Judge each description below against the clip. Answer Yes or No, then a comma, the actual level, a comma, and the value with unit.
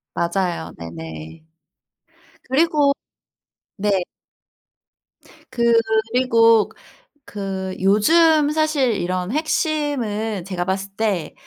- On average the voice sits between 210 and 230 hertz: Yes, high, 220 Hz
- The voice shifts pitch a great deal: Yes, wide, 6.8 semitones